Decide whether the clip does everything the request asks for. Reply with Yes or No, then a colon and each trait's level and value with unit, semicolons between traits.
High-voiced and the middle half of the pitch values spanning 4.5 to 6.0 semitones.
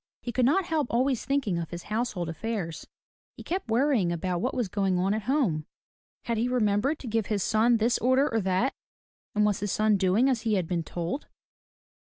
Yes: high, 220 Hz; average, 5.1 semitones